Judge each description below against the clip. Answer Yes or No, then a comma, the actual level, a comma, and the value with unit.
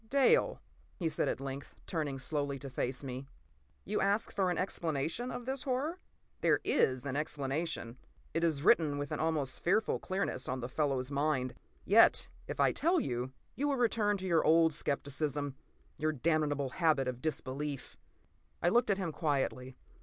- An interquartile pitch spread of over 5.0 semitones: Yes, wide, 5.6 semitones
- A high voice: No, medium, 150 Hz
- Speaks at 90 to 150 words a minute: No, average, 170 wpm